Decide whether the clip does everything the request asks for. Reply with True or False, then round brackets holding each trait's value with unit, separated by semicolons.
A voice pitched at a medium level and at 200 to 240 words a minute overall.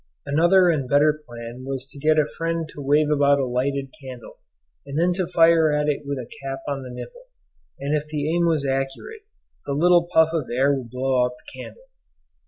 True (145 Hz; 205 wpm)